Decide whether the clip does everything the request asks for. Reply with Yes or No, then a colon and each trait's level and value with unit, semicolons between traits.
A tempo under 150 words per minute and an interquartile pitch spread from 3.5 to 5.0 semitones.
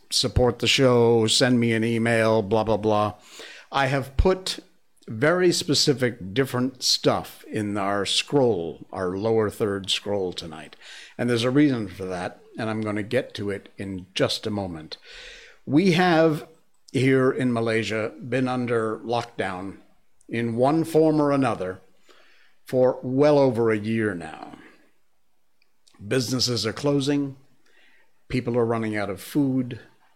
Yes: average, 140 wpm; average, 4.1 semitones